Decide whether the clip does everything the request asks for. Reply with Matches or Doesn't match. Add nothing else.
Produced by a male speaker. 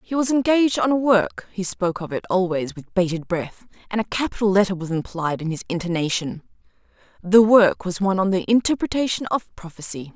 Doesn't match